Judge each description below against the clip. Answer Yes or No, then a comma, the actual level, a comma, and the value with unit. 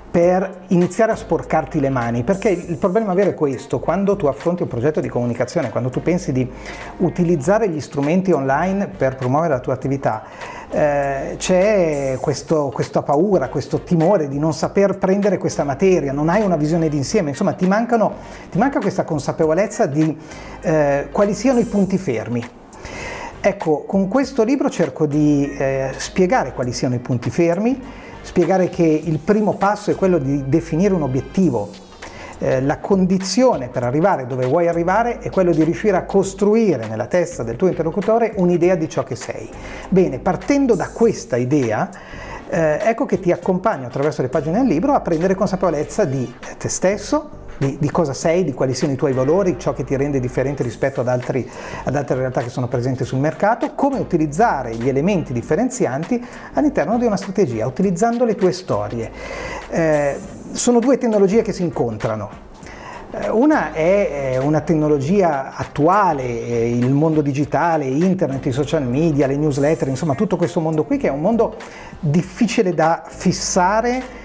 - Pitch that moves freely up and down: Yes, wide, 5.8 semitones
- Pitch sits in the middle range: Yes, medium, 165 Hz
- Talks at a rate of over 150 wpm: Yes, average, 165 wpm